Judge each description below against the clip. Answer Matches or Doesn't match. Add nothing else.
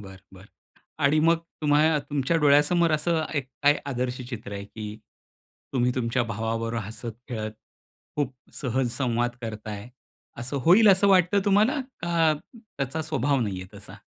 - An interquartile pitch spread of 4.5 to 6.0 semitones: Matches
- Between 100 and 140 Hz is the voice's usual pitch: Matches